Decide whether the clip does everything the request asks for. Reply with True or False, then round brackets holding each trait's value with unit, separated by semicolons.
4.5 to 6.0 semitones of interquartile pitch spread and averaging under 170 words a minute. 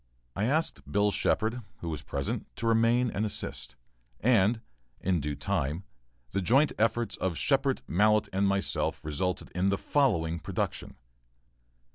True (5.2 semitones; 140 wpm)